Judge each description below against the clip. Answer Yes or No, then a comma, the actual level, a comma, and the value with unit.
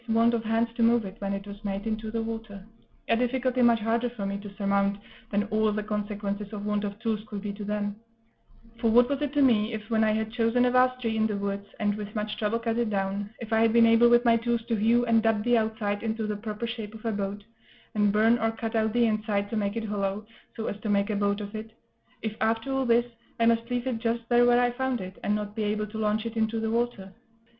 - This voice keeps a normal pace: No, fast, 265 wpm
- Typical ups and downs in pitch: No, narrow, 2.0 semitones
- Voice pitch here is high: Yes, high, 220 Hz